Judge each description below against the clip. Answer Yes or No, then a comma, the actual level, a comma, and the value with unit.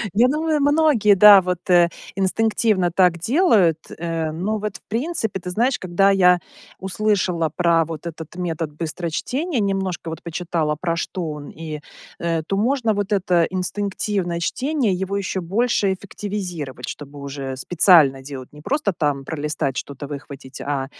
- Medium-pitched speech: Yes, medium, 180 Hz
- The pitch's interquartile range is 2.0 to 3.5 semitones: No, average, 4.3 semitones